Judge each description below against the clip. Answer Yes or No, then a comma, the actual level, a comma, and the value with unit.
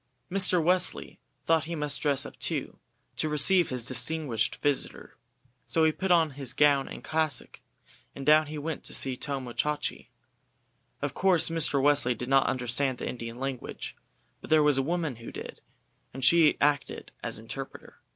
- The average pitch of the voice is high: No, medium, 145 Hz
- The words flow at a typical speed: Yes, average, 170 wpm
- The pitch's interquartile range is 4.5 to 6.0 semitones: No, average, 3.2 semitones